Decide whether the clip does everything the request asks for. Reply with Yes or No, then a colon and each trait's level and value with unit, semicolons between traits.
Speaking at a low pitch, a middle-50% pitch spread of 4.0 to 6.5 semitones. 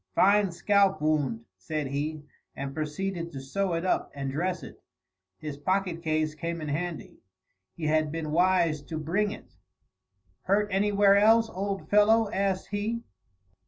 No: medium, 170 Hz; average, 4.4 semitones